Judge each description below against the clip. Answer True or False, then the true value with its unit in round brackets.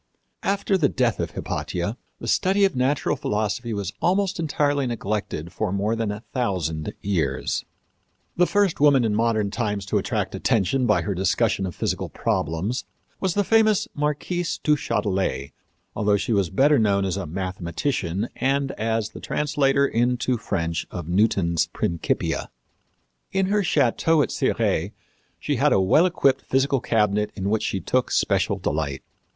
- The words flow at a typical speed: True (155 wpm)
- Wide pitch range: True (6.7 semitones)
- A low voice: True (115 Hz)